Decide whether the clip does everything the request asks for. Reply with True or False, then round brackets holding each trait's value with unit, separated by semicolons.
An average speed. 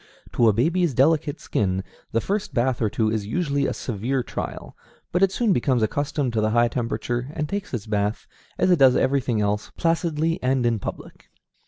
True (190 wpm)